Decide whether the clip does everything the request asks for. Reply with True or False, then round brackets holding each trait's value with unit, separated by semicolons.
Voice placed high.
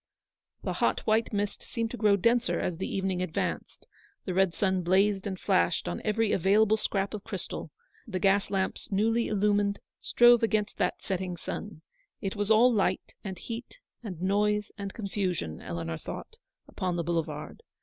True (200 Hz)